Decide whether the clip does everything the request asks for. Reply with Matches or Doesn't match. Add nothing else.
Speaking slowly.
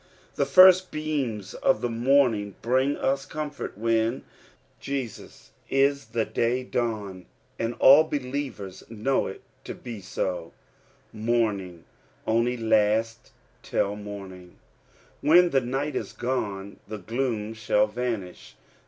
Matches